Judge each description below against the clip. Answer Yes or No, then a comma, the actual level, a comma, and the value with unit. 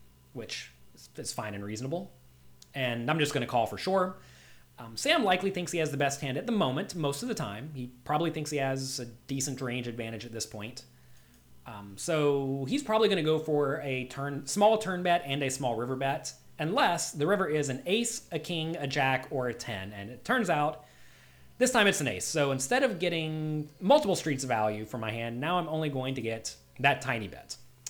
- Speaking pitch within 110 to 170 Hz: Yes, low, 135 Hz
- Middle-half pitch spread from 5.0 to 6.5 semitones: Yes, wide, 5.6 semitones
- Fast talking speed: Yes, fast, 215 wpm